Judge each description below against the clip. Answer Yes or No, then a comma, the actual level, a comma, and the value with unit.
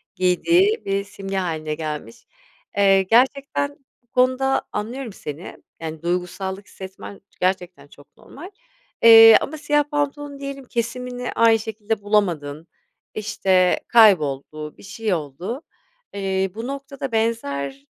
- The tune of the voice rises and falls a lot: Yes, wide, 5.9 semitones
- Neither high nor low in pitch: No, high, 205 Hz